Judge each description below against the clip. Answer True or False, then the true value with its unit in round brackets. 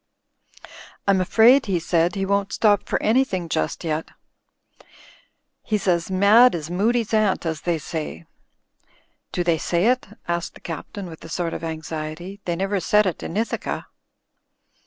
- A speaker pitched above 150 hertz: True (185 Hz)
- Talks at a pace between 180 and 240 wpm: False (155 wpm)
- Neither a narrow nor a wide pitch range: True (3.8 semitones)